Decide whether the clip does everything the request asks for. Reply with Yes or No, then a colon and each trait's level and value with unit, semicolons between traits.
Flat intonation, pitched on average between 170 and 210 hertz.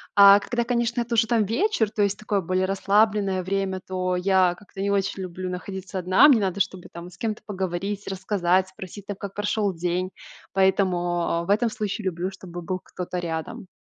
Yes: narrow, 2.0 semitones; high, 190 Hz